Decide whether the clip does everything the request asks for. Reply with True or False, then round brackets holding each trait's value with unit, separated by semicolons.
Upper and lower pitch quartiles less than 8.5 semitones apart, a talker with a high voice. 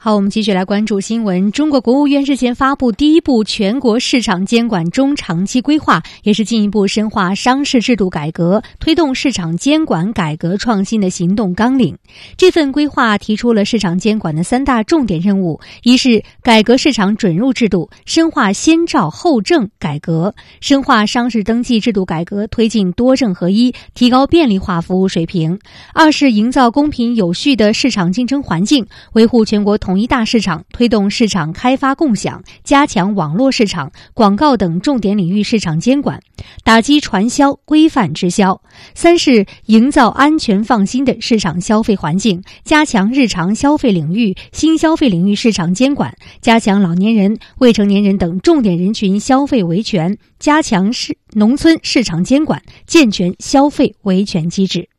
True (5.5 semitones; 225 Hz)